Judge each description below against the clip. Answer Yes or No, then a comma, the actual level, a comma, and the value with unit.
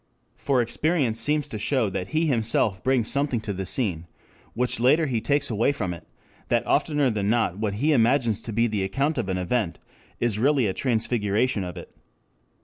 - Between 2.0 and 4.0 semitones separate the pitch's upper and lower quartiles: No, average, 5.0 semitones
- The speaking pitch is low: Yes, low, 115 Hz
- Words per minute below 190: No, average, 195 wpm